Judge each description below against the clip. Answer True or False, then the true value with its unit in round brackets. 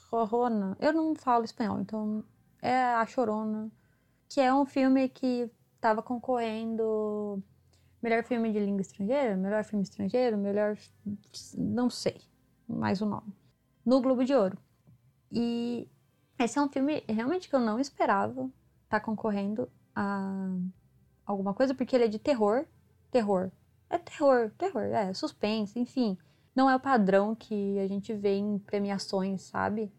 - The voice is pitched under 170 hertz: False (220 Hz)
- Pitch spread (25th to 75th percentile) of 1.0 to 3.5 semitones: False (3.9 semitones)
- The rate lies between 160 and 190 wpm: False (150 wpm)